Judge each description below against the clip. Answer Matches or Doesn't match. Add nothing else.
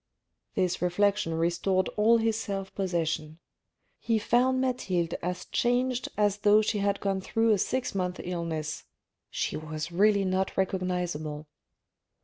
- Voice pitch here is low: Doesn't match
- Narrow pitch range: Doesn't match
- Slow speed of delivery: Matches